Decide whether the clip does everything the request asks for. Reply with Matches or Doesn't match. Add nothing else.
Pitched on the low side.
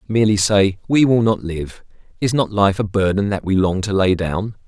Matches